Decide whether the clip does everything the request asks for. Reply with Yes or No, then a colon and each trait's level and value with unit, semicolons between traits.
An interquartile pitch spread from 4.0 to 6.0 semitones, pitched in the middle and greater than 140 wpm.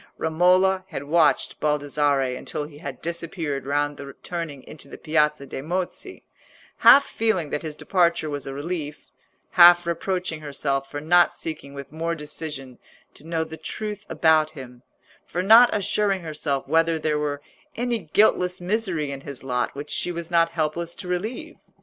No: average, 3.5 semitones; medium, 160 Hz; average, 160 wpm